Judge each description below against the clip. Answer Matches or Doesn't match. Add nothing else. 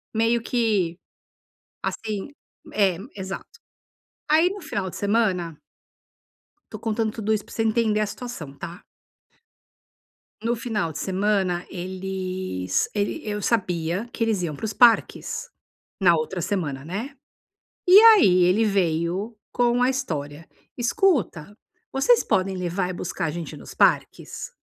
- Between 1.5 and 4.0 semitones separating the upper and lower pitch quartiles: Doesn't match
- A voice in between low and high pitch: Doesn't match